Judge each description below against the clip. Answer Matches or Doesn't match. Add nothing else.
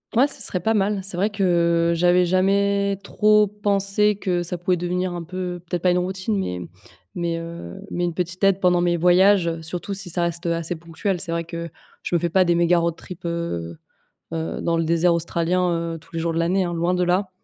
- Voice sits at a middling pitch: Matches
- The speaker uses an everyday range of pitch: Doesn't match